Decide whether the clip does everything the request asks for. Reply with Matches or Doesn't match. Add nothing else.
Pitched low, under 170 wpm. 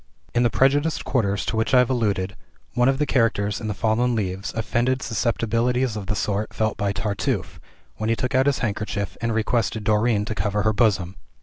Doesn't match